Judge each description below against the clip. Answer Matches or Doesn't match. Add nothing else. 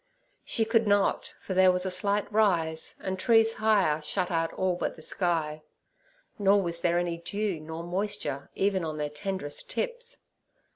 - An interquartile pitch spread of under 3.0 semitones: Doesn't match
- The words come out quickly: Doesn't match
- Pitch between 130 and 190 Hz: Matches